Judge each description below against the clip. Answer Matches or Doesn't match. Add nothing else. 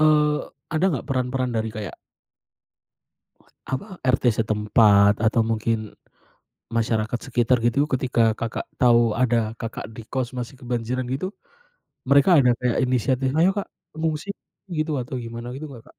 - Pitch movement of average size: Matches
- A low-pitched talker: Matches